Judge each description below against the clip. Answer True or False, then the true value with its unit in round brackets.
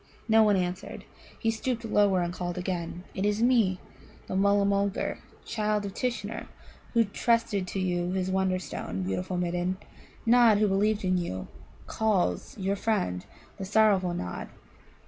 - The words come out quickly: False (145 wpm)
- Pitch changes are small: False (3.1 semitones)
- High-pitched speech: True (195 Hz)